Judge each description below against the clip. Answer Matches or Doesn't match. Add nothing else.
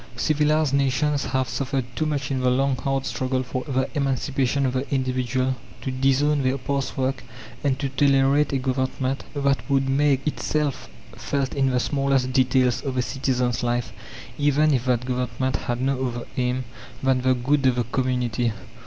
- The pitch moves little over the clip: Matches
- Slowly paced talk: Doesn't match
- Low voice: Matches